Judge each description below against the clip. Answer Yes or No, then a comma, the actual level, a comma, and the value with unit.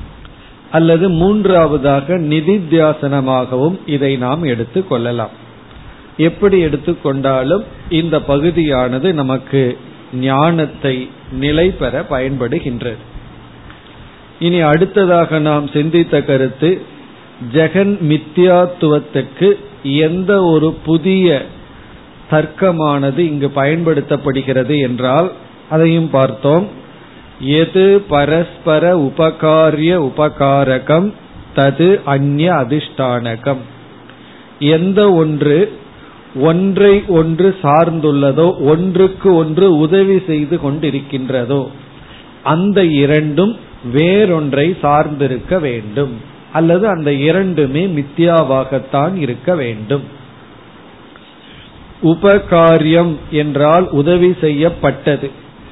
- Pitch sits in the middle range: Yes, medium, 155 Hz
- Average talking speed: No, slow, 70 wpm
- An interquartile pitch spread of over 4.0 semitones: No, average, 3.7 semitones